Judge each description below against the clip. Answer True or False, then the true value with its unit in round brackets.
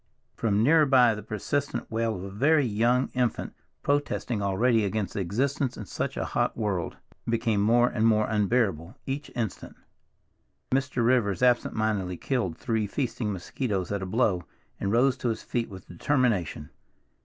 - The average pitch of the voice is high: False (115 Hz)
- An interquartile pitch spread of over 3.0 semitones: True (3.9 semitones)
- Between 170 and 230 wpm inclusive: False (155 wpm)